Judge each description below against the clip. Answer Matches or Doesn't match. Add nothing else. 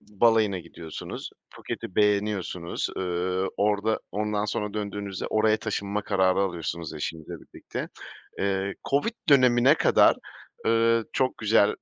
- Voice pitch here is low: Matches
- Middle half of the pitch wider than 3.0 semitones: Doesn't match